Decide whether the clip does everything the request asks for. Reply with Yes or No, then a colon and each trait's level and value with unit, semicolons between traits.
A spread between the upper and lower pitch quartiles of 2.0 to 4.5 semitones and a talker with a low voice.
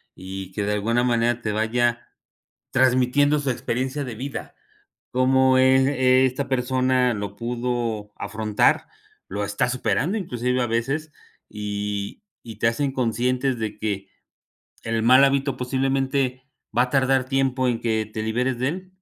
Yes: average, 2.9 semitones; low, 125 Hz